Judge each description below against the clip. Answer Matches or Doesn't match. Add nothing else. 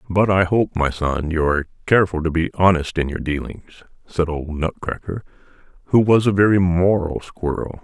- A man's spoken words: Matches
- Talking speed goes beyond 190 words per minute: Doesn't match